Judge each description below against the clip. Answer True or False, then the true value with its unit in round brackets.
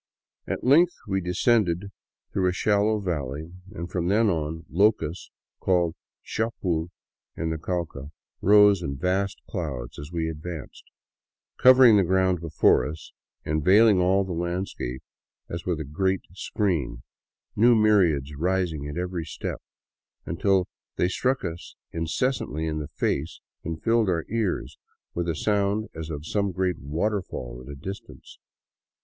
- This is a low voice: True (90 Hz)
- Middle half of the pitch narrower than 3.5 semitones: False (4.0 semitones)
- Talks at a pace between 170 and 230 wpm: False (145 wpm)